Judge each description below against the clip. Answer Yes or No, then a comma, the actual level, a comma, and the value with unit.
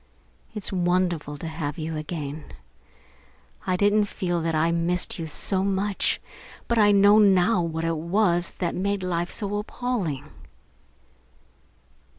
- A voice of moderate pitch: Yes, medium, 180 Hz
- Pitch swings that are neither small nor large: Yes, average, 3.6 semitones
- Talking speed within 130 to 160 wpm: Yes, average, 140 wpm